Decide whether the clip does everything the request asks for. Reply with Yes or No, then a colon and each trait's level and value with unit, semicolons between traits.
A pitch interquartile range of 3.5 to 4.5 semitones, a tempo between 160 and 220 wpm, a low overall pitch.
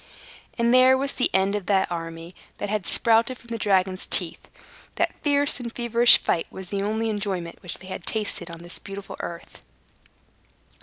No: average, 4.1 semitones; average, 175 wpm; high, 205 Hz